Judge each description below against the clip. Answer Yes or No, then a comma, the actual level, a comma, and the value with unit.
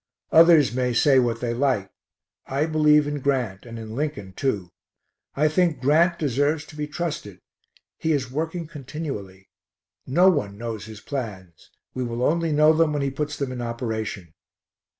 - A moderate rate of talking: Yes, average, 165 wpm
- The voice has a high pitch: No, low, 135 Hz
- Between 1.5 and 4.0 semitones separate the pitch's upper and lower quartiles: No, average, 4.8 semitones